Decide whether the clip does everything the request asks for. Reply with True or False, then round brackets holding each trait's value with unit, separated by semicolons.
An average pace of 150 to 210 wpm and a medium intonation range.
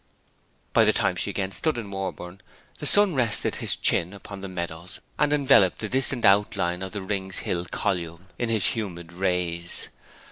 True (175 wpm; 3.9 semitones)